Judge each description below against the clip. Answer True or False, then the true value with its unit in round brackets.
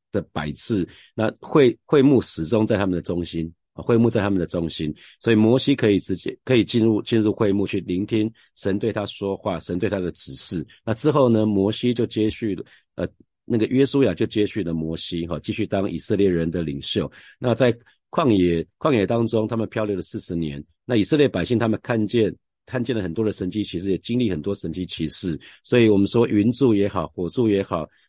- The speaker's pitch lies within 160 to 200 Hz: False (105 Hz)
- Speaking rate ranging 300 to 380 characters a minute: True (310 characters per minute)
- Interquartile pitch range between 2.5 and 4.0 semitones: False (4.6 semitones)